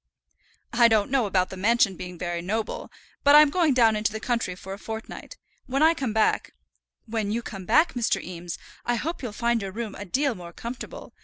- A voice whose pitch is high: Yes, high, 225 Hz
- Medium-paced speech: No, fast, 215 wpm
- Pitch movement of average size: Yes, average, 4.2 semitones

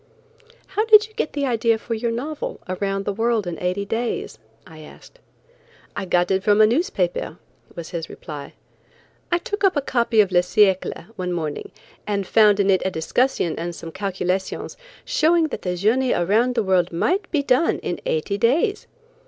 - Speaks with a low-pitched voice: No, high, 210 Hz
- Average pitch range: No, wide, 6.8 semitones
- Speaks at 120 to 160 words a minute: No, average, 180 wpm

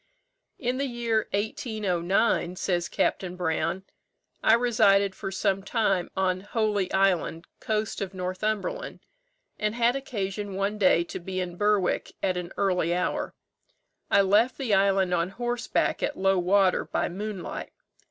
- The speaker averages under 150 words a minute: Yes, average, 140 wpm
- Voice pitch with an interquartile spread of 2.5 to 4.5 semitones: Yes, average, 2.9 semitones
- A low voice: No, high, 195 Hz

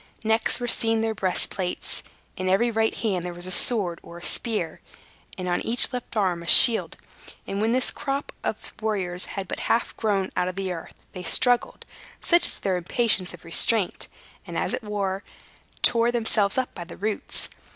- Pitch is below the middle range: No, high, 205 Hz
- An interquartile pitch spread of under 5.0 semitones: Yes, average, 4.0 semitones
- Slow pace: No, average, 195 wpm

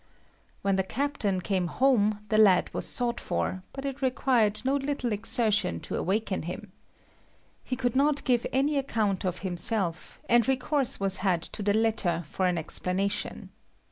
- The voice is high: Yes, high, 215 Hz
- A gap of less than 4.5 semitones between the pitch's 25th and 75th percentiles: No, wide, 5.4 semitones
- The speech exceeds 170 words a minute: No, average, 160 wpm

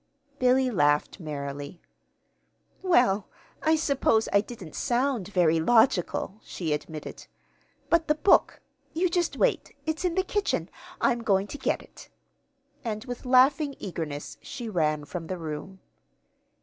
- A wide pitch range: Yes, wide, 9.0 semitones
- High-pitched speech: Yes, high, 220 Hz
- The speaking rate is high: No, slow, 135 wpm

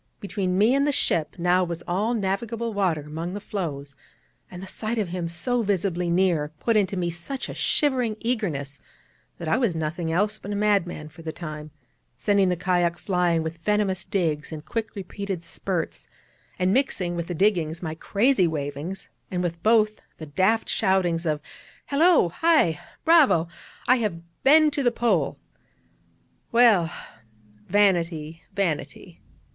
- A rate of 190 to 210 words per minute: No, average, 155 wpm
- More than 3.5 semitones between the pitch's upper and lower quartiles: Yes, average, 4.3 semitones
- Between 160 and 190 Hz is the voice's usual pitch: Yes, medium, 185 Hz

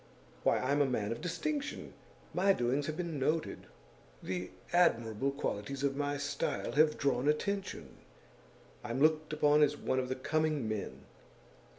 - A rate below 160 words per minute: Yes, average, 150 wpm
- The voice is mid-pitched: Yes, medium, 145 Hz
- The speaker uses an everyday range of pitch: Yes, average, 3.5 semitones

